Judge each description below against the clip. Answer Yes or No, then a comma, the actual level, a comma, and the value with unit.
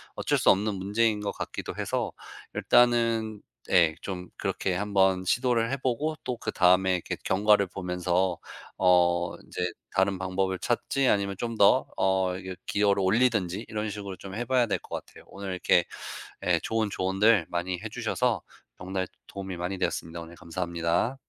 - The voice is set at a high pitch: No, very low, 95 Hz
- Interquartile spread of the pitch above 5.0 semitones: No, average, 3.1 semitones